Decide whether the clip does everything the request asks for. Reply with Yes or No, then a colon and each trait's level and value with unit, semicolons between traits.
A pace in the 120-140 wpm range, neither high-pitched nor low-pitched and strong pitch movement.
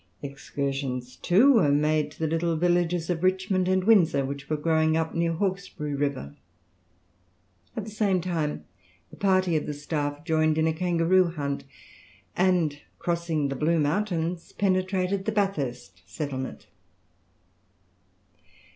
No: slow, 135 wpm; medium, 165 Hz; average, 4.1 semitones